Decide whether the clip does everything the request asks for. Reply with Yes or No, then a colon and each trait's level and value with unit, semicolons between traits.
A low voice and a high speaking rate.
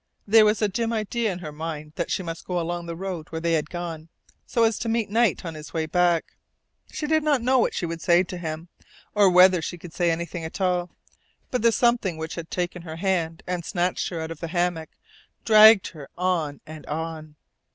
No: medium, 175 Hz; fast, 225 wpm